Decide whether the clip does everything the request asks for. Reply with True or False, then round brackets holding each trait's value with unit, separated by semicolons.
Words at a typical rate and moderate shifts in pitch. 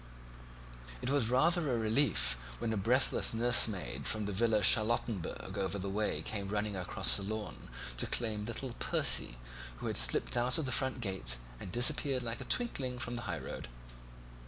True (175 wpm; 4.0 semitones)